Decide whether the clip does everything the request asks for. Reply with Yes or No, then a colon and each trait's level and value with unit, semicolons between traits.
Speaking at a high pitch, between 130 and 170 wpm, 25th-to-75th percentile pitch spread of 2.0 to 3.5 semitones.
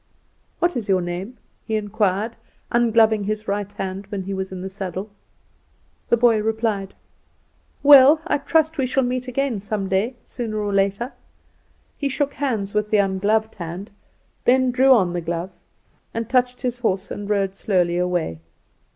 No: high, 210 Hz; average, 160 wpm; average, 4.2 semitones